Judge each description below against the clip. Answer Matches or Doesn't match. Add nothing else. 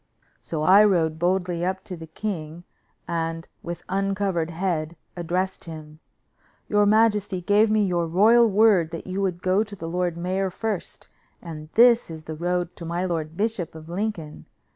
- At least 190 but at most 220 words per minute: Doesn't match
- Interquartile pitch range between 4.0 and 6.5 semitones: Doesn't match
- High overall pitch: Doesn't match